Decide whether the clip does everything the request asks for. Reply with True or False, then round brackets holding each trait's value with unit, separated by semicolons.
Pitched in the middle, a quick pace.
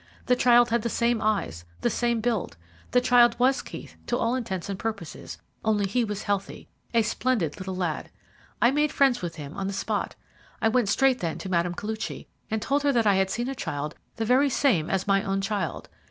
False (220 Hz; 210 wpm)